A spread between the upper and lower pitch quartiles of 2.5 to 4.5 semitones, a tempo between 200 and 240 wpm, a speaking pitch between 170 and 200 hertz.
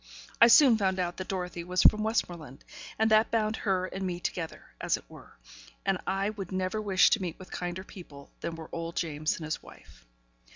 Yes: average, 3.3 semitones; fast, 205 wpm; medium, 185 Hz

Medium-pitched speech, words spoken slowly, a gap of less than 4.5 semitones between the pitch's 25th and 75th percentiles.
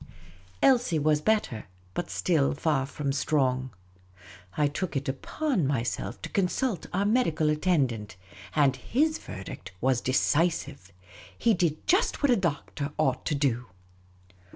No: medium, 150 Hz; slow, 130 wpm; wide, 5.6 semitones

